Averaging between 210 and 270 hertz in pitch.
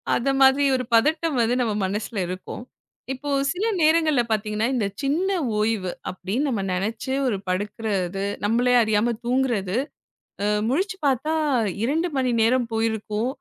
Yes: high, 235 Hz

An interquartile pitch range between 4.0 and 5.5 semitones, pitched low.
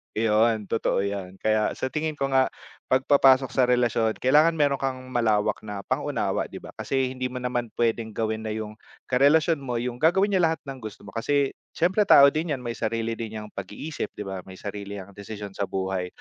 Yes: average, 4.3 semitones; low, 120 Hz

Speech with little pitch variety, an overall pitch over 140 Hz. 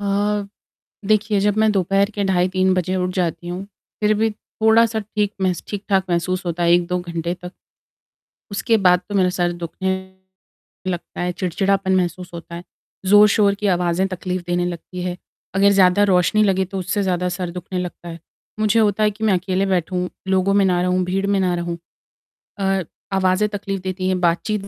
Yes: narrow, 2.1 semitones; medium, 185 Hz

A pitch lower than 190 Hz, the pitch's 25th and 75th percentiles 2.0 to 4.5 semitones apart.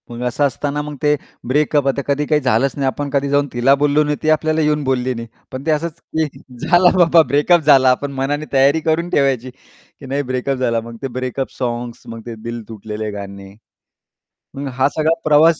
Yes: medium, 140 Hz; average, 3.1 semitones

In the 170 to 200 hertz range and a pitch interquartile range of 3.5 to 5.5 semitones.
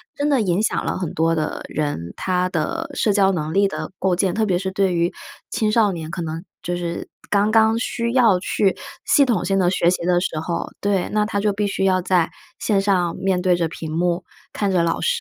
No: medium, 185 Hz; average, 3.1 semitones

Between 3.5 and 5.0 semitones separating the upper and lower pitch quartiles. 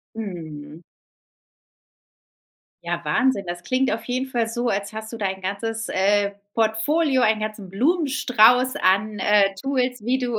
Yes: average, 4.0 semitones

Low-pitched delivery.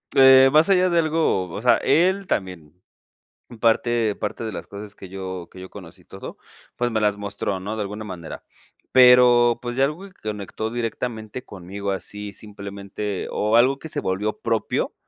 Yes: low, 110 Hz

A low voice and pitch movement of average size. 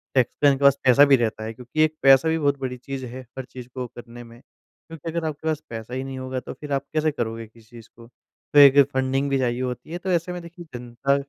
Yes: low, 130 Hz; average, 3.2 semitones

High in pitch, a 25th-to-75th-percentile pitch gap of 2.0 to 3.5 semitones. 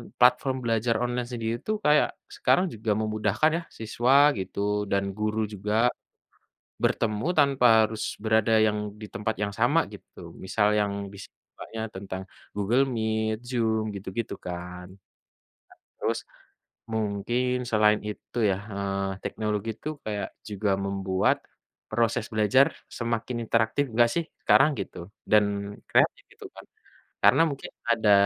No: low, 110 Hz; average, 2.7 semitones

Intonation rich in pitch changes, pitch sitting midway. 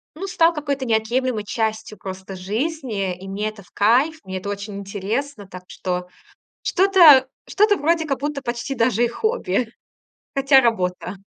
No: wide, 6.1 semitones; high, 230 Hz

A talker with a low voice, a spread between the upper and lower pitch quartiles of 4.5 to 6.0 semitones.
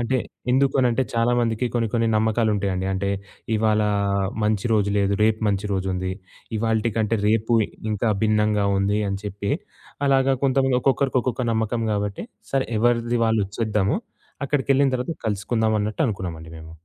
No: low, 110 Hz; average, 2.9 semitones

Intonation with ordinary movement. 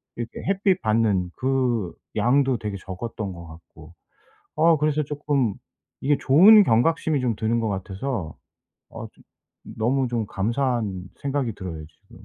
No: wide, 6.1 semitones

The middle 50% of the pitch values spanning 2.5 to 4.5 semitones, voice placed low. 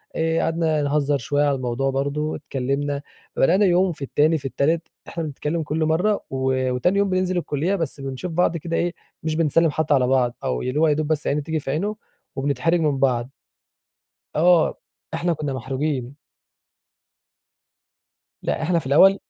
No: average, 3.4 semitones; medium, 150 Hz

